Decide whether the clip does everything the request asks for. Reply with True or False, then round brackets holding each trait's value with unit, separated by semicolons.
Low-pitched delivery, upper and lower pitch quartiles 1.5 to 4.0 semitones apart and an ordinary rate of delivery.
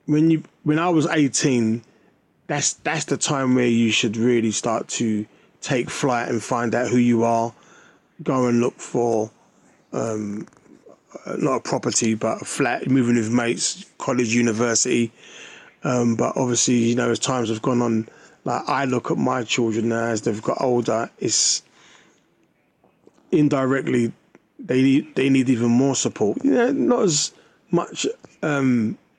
True (120 Hz; 2.6 semitones; 155 wpm)